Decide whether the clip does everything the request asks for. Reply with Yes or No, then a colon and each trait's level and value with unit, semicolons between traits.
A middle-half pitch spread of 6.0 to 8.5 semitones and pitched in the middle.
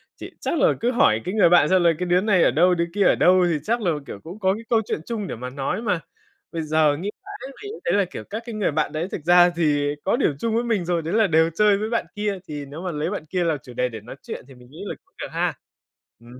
No: average, 5.3 semitones; medium, 175 Hz